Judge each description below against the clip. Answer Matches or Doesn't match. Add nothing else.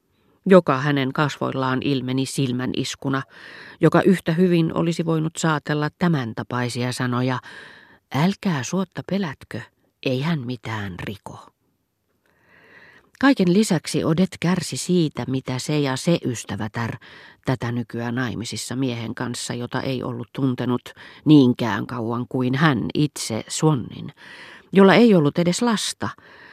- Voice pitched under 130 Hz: Doesn't match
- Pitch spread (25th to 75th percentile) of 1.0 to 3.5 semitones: Doesn't match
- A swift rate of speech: Doesn't match